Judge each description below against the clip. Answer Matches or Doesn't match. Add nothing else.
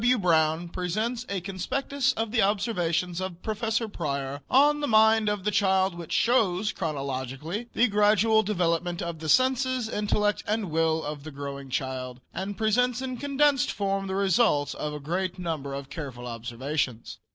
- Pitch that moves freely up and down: Matches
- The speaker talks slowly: Doesn't match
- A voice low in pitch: Doesn't match